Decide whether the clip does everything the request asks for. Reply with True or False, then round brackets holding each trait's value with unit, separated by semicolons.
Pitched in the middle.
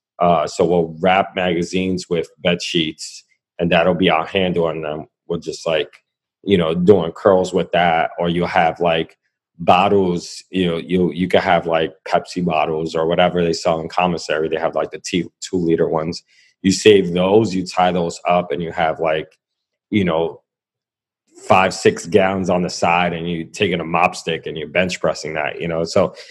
False (90 Hz)